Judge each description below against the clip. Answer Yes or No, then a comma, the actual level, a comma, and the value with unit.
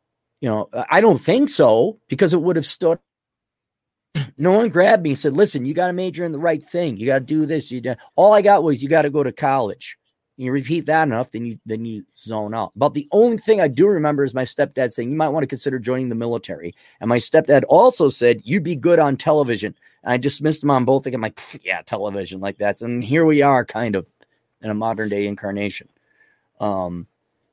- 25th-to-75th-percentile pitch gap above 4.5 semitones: Yes, wide, 5.6 semitones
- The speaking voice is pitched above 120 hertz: Yes, low, 135 Hz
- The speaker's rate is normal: No, fast, 240 wpm